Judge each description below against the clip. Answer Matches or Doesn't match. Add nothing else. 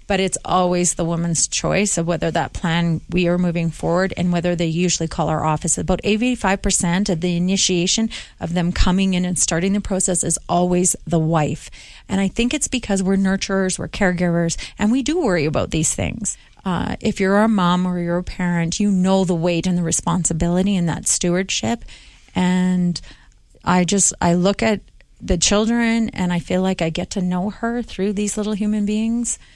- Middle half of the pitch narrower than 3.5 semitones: Matches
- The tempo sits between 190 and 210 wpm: Matches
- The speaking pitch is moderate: Matches